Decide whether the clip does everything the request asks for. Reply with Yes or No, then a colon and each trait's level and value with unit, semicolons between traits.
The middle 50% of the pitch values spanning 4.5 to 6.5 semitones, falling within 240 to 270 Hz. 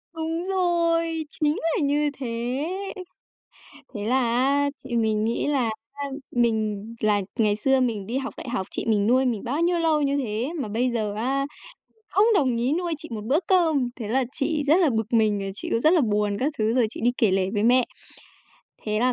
Yes: average, 5.3 semitones; very high, 250 Hz